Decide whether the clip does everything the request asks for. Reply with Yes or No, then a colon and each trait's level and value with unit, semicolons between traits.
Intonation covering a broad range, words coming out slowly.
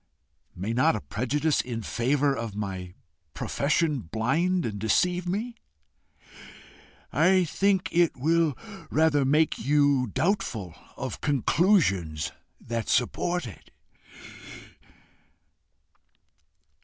Yes: wide, 7.0 semitones; slow, 95 wpm